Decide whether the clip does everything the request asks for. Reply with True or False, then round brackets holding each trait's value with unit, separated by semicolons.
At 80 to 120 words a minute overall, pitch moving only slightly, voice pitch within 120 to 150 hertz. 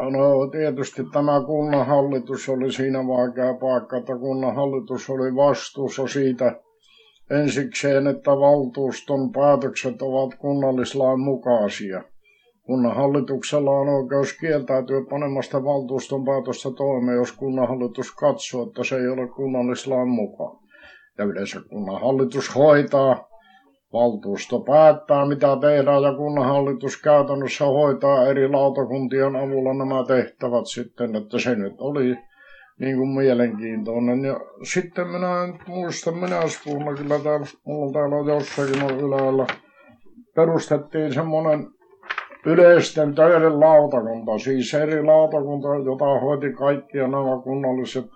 True (110 wpm; 2.1 semitones; 135 Hz)